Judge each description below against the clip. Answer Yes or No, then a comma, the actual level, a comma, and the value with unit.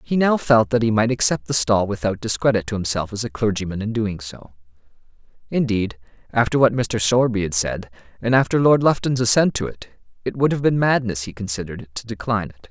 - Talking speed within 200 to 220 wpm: Yes, fast, 205 wpm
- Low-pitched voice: Yes, low, 110 Hz